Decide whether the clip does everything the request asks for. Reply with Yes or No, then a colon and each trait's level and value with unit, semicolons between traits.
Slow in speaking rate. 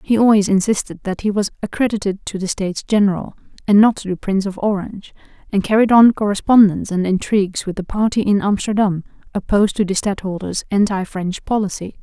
No: average, 180 wpm